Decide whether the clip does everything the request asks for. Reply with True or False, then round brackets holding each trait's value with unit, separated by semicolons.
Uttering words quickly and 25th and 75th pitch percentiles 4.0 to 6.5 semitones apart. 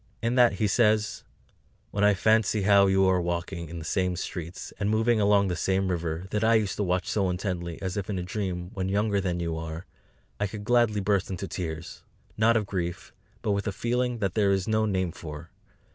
False (215 wpm; 3.0 semitones)